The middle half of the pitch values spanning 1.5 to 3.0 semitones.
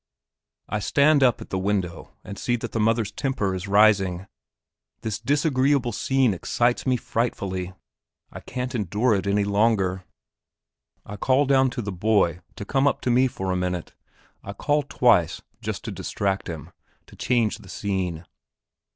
No: average, 4.9 semitones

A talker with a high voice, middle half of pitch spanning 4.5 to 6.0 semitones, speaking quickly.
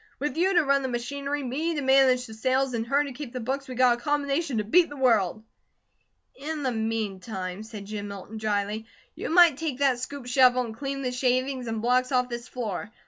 No: very high, 255 Hz; average, 3.8 semitones; fast, 215 wpm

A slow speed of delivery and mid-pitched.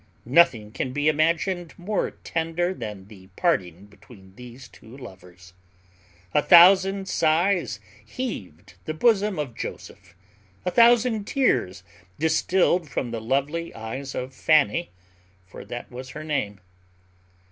Yes: slow, 125 wpm; medium, 145 Hz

